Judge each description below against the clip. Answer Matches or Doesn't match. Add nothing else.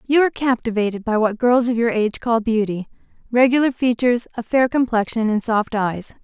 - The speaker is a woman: Matches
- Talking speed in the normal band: Matches